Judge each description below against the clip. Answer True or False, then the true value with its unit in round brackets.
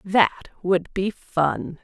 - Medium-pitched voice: True (180 Hz)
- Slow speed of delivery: True (130 wpm)